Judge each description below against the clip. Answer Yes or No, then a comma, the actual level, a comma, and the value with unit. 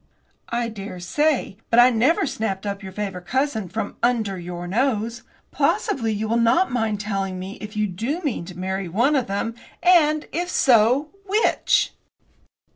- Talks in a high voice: Yes, high, 220 Hz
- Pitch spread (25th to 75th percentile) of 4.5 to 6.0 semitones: Yes, average, 5.1 semitones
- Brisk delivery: No, average, 160 wpm